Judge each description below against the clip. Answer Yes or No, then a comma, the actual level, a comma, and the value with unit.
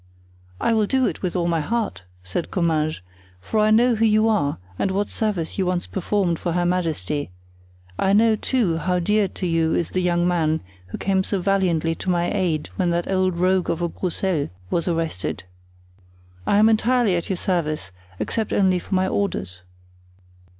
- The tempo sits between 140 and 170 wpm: No, average, 185 wpm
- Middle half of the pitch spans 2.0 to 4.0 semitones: Yes, average, 3.4 semitones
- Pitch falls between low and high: Yes, medium, 180 Hz